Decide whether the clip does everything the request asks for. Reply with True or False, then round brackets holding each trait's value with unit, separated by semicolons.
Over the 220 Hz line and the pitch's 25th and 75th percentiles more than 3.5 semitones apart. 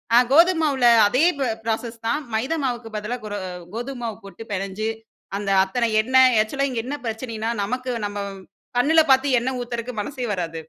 False (240 Hz; 3.2 semitones)